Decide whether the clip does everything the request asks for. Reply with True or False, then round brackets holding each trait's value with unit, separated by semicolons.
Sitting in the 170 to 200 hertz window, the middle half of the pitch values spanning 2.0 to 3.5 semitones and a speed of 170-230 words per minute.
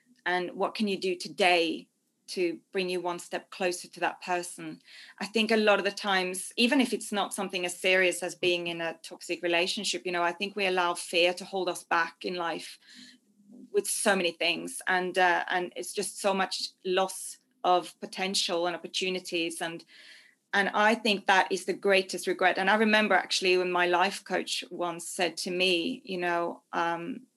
True (185 Hz; 2.4 semitones; 195 wpm)